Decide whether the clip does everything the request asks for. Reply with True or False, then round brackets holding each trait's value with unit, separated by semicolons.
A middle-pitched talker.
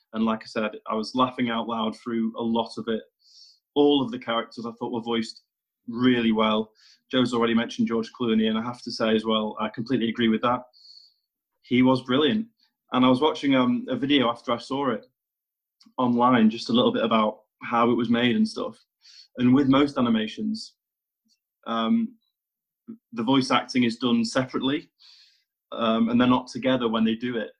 False (120 Hz)